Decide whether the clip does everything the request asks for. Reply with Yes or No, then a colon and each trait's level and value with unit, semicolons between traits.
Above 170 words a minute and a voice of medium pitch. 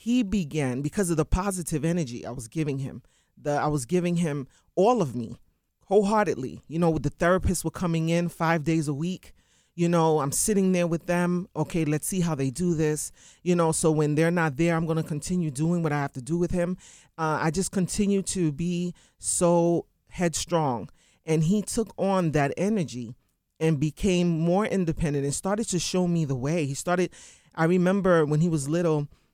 Yes: average, 200 wpm; medium, 165 Hz